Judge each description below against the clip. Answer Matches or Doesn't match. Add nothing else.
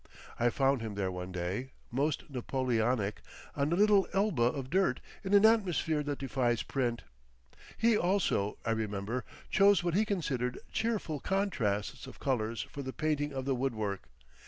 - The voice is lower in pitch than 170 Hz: Matches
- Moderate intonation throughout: Doesn't match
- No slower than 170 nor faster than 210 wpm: Doesn't match